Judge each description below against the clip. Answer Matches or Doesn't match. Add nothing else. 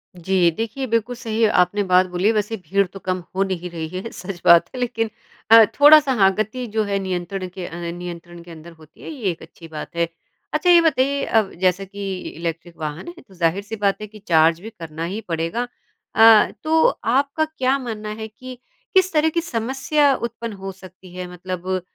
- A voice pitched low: Doesn't match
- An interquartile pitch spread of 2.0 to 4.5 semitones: Doesn't match